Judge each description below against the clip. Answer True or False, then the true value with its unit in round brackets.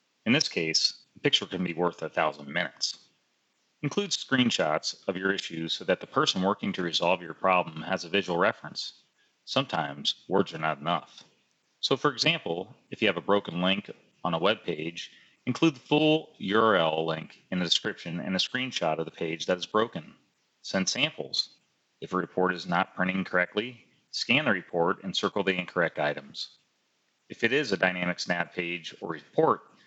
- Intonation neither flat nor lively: True (4.0 semitones)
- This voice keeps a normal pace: True (180 wpm)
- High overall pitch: False (95 Hz)